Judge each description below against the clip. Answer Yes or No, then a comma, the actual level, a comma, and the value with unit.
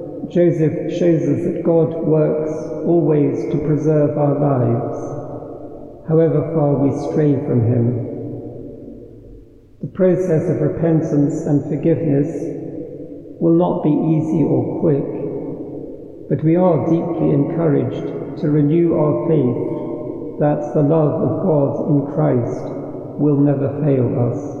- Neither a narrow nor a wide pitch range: No, narrow, 1.8 semitones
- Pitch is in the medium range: Yes, medium, 150 Hz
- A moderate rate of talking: No, slow, 120 wpm